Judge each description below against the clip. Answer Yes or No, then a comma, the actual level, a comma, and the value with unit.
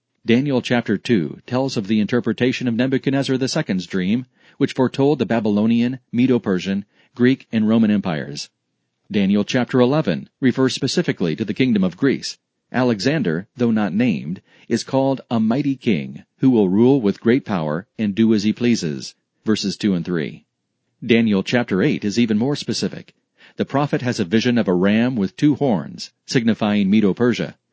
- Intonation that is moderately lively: Yes, average, 3.8 semitones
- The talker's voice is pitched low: Yes, low, 120 Hz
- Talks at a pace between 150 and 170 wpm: Yes, average, 160 wpm